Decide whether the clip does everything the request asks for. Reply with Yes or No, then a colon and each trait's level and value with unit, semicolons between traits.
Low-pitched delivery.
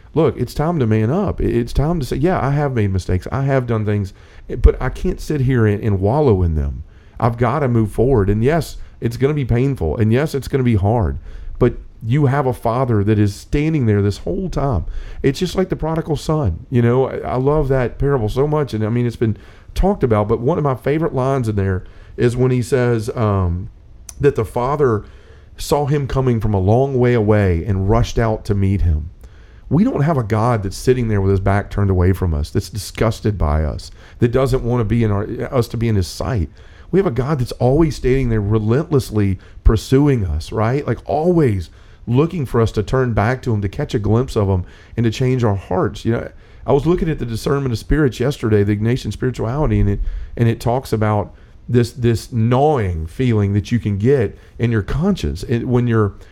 Yes: low, 115 Hz